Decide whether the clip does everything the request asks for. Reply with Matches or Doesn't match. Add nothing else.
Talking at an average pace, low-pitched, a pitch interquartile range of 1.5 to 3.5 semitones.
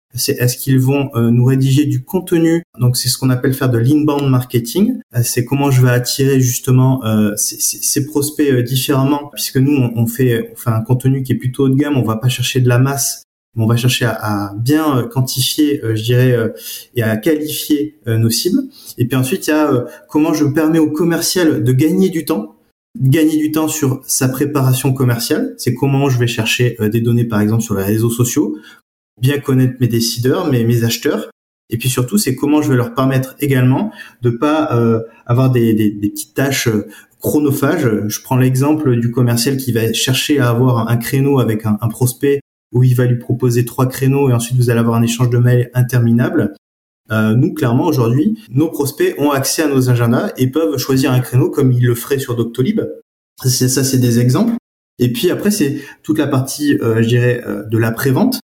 Matches